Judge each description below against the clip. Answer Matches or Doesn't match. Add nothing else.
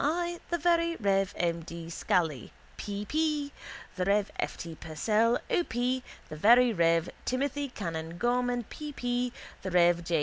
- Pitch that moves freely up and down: Matches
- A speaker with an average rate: Matches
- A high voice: Matches